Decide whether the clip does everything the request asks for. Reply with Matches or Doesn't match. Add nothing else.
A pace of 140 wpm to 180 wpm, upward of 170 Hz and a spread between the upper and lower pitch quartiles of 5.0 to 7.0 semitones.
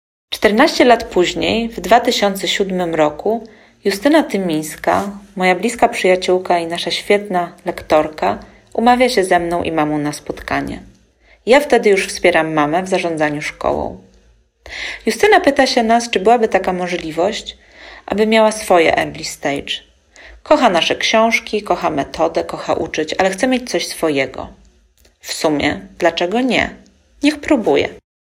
Doesn't match